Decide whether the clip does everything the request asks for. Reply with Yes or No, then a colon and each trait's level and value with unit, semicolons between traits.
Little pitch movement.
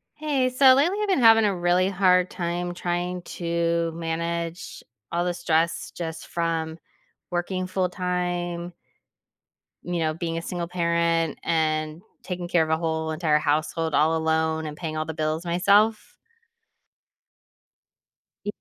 Yes: narrow, 2.0 semitones